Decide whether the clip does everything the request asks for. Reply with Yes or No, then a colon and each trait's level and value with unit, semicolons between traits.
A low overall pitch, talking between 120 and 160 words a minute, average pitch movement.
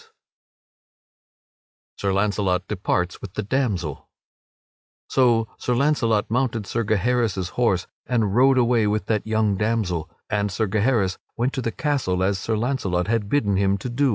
Yes: low, 110 Hz; average, 155 wpm; average, 3.8 semitones